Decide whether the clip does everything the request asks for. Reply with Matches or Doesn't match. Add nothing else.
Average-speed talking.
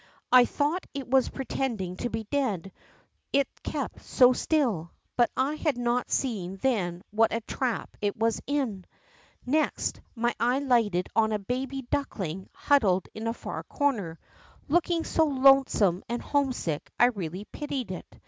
Matches